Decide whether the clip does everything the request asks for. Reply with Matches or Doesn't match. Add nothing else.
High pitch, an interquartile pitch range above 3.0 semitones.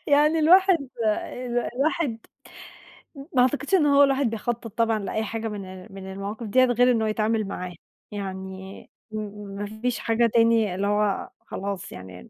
Matches